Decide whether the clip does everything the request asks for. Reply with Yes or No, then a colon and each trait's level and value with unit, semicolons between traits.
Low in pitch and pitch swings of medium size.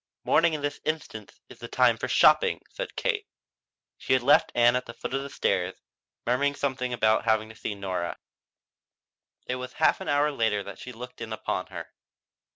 Yes: low, 125 Hz; average, 4.6 semitones